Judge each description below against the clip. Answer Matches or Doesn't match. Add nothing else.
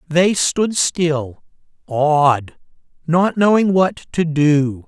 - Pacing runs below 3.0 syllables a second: Matches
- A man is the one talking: Matches